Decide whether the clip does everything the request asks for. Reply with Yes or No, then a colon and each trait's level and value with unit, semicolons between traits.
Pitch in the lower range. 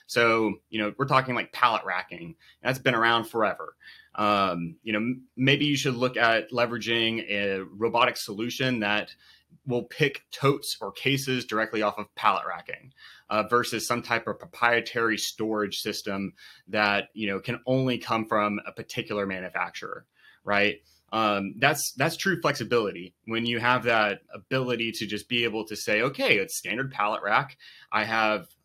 Yes: low, 115 Hz